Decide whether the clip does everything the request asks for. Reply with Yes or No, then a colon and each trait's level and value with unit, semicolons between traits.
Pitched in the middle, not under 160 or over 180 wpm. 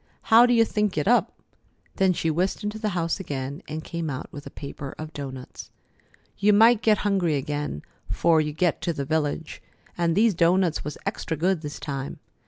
No: medium, 165 Hz; average, 190 wpm